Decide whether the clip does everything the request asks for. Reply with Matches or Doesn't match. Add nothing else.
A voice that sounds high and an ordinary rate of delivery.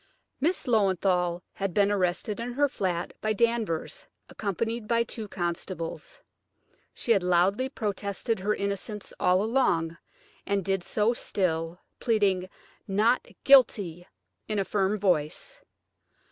Doesn't match